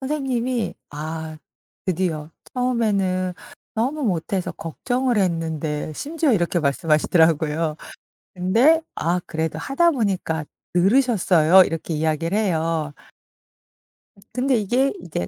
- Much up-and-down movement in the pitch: Yes, wide, 7.2 semitones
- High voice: No, medium, 180 Hz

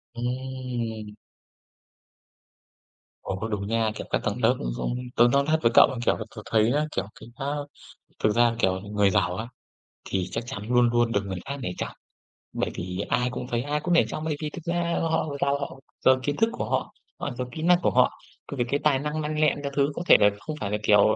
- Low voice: Yes, low, 125 Hz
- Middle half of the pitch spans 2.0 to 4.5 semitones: No, average, 5.3 semitones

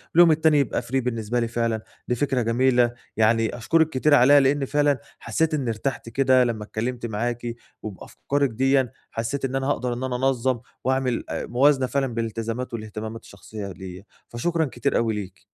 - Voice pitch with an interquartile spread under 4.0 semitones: Yes, average, 2.9 semitones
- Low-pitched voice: Yes, low, 125 Hz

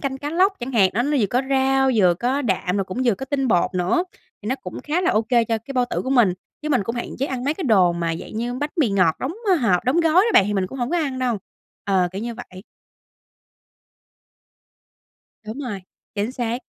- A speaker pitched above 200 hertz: Yes, high, 240 Hz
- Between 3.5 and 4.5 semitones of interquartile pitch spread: No, average, 5.2 semitones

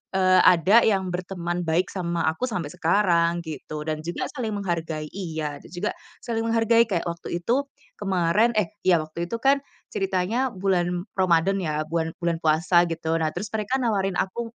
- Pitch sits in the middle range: Yes, medium, 180 Hz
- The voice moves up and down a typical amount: Yes, average, 3.6 semitones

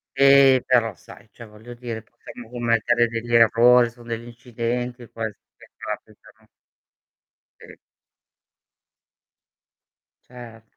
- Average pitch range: No, narrow, 1.2 semitones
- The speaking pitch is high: No, low, 120 Hz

